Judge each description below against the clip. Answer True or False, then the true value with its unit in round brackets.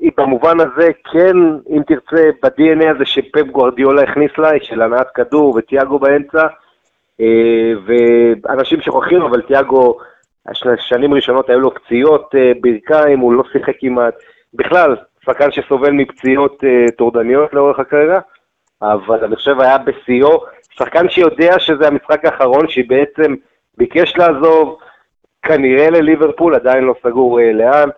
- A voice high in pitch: False (140 Hz)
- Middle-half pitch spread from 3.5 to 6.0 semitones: True (3.8 semitones)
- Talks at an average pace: True (120 wpm)